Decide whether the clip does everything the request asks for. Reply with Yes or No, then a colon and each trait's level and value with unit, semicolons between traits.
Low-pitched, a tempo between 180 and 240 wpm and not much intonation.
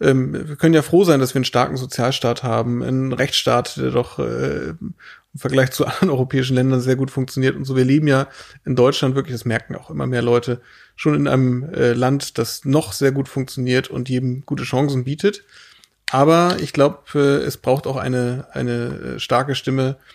Yes: low, 130 Hz; average, 185 wpm; narrow, 1.7 semitones